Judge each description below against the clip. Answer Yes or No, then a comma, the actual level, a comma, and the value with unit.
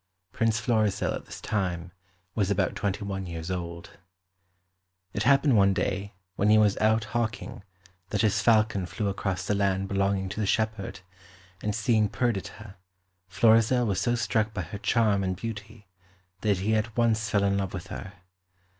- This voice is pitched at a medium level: No, low, 105 Hz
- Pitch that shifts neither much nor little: No, narrow, 2.2 semitones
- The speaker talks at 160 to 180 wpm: Yes, average, 165 wpm